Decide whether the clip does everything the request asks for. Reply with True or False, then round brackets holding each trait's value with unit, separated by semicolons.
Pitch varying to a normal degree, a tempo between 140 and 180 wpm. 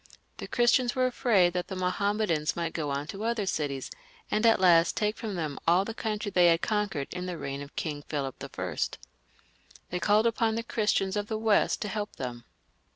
False (4.7 semitones; 205 wpm)